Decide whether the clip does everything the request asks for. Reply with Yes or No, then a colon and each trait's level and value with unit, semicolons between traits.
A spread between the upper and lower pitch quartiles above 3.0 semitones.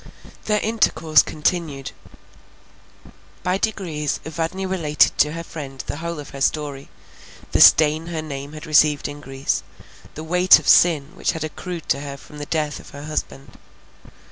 No: narrow, 2.6 semitones